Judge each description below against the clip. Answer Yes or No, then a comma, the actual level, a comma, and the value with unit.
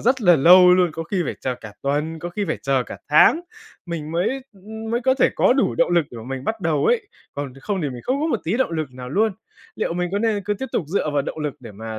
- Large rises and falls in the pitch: Yes, wide, 6.6 semitones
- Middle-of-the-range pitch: Yes, medium, 170 Hz